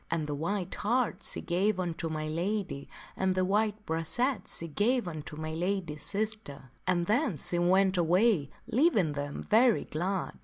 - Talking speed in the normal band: Yes, average, 160 wpm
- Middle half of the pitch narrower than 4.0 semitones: No, average, 4.7 semitones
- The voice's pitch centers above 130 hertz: Yes, medium, 185 Hz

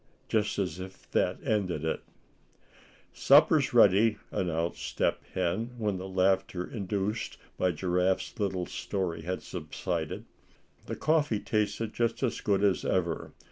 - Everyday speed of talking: No, slow, 130 wpm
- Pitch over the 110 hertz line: No, very low, 95 Hz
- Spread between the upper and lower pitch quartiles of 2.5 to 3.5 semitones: Yes, average, 2.9 semitones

